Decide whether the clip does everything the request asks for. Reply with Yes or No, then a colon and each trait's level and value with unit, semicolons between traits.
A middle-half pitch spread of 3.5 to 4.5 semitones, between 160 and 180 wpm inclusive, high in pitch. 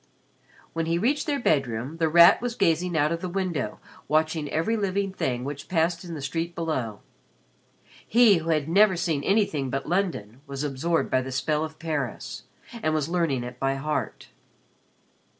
No: average, 4.1 semitones; average, 170 wpm; medium, 160 Hz